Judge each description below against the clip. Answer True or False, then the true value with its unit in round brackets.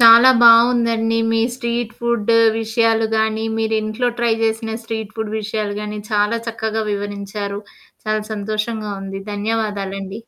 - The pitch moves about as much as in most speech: False (1.6 semitones)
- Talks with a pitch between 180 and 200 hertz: False (220 Hz)